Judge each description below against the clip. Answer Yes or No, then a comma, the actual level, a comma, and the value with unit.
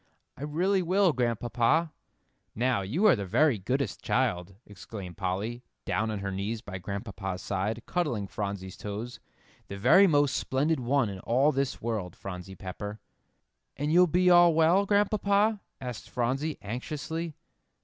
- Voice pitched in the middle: No, low, 120 Hz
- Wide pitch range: Yes, wide, 8.1 semitones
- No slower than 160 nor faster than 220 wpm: No, average, 145 wpm